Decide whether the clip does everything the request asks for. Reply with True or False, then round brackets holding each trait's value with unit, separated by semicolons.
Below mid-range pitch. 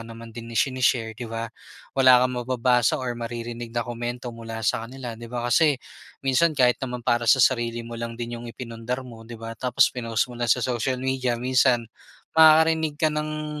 True (120 Hz)